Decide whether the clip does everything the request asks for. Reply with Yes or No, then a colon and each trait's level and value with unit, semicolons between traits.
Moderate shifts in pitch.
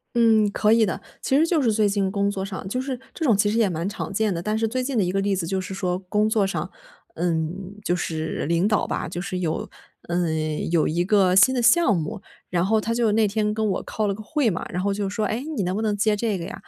Yes: average, 3.3 semitones